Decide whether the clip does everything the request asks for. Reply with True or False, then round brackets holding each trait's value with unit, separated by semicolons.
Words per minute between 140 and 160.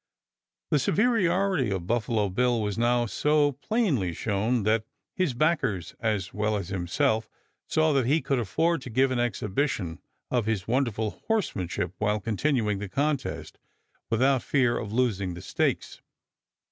True (145 wpm)